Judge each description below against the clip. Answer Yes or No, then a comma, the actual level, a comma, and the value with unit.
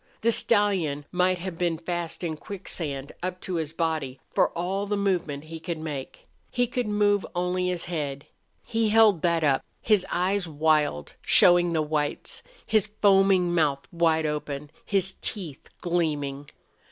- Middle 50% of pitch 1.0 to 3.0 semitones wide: No, average, 4.0 semitones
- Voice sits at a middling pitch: Yes, medium, 175 Hz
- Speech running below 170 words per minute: Yes, average, 150 wpm